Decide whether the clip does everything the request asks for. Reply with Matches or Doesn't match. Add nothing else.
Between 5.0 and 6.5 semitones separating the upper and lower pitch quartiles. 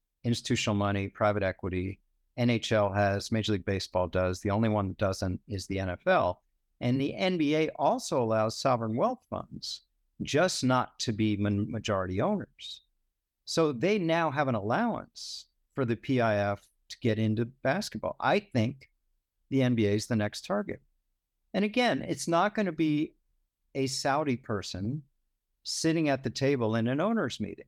Matches